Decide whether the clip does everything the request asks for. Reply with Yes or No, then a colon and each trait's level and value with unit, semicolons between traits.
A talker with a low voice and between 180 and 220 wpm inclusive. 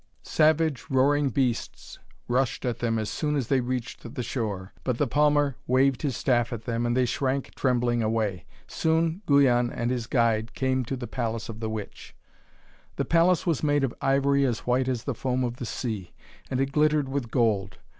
Yes: low, 125 Hz; average, 190 wpm